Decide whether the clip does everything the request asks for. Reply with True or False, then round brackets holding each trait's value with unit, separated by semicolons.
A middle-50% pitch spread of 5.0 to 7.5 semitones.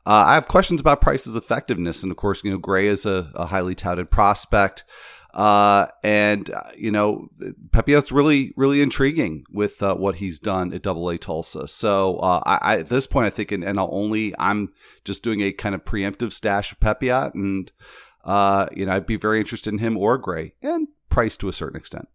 False (2.8 semitones)